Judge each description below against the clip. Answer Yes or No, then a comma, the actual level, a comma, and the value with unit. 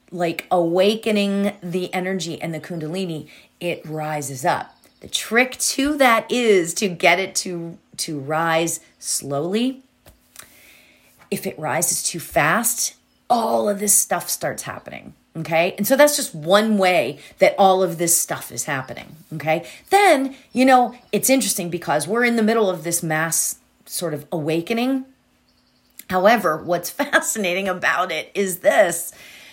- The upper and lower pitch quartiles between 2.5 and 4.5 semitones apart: No, average, 5.3 semitones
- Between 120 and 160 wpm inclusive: Yes, average, 145 wpm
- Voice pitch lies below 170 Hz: No, medium, 185 Hz